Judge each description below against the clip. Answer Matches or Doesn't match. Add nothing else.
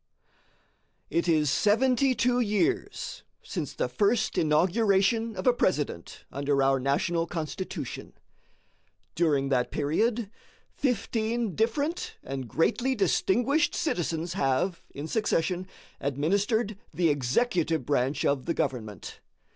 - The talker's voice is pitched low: Doesn't match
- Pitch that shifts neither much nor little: Doesn't match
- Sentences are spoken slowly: Matches